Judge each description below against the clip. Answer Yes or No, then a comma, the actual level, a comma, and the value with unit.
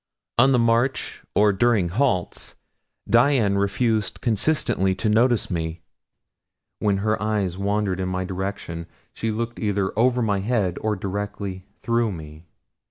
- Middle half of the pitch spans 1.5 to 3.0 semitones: No, average, 3.7 semitones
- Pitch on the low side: Yes, low, 105 Hz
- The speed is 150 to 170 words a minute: No, slow, 135 wpm